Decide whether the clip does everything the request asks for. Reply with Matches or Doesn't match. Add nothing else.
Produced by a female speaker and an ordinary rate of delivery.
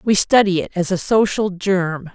Matches